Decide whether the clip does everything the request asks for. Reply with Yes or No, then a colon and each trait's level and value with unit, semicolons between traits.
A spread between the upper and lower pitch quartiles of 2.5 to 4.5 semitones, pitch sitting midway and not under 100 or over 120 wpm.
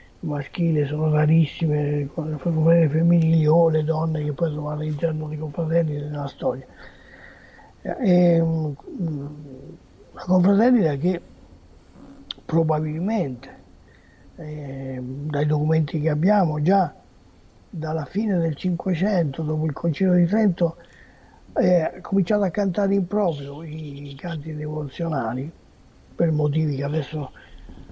Yes: average, 2.8 semitones; medium, 155 Hz; slow, 115 wpm